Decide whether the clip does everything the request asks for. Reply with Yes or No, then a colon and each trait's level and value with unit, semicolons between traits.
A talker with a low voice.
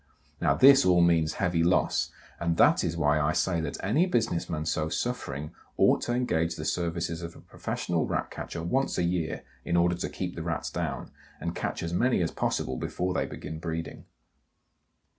Yes: very low, 85 Hz